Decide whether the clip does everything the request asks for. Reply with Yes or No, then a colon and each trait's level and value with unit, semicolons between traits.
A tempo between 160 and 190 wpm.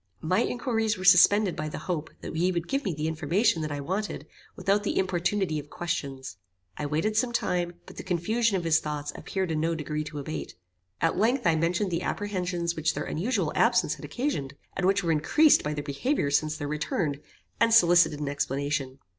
No: average, 200 wpm